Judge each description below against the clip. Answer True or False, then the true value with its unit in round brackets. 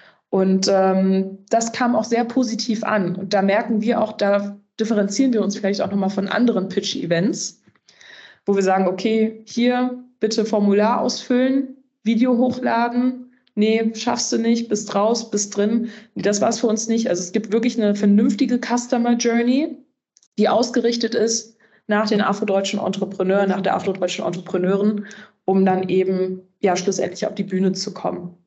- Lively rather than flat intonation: False (3.3 semitones)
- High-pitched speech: True (215 Hz)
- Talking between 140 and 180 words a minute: True (160 wpm)